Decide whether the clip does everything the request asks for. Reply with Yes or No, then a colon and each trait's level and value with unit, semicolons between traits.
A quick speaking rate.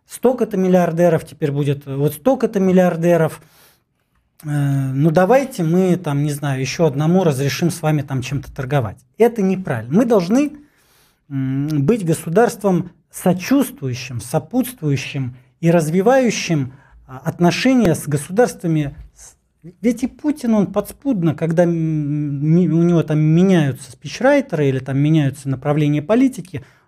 No: average, 120 wpm